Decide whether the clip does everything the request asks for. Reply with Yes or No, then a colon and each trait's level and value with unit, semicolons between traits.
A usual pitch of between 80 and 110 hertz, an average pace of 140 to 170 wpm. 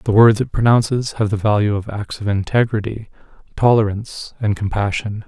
Yes: low, 105 Hz; average, 160 wpm